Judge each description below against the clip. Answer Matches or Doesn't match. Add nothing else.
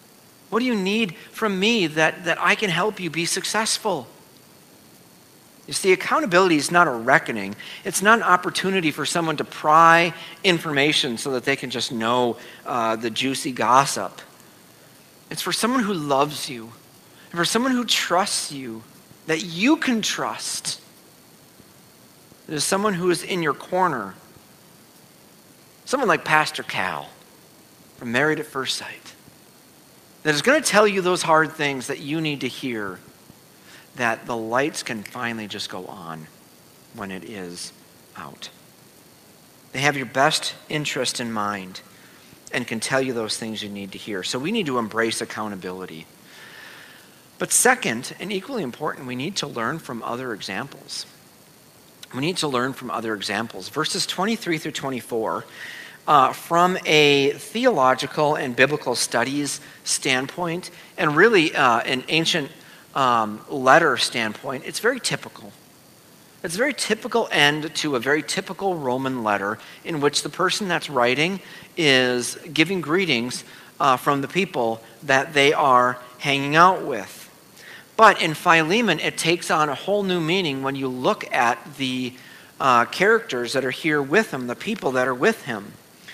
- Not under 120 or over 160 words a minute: Matches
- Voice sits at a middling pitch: Matches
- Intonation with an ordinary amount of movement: Doesn't match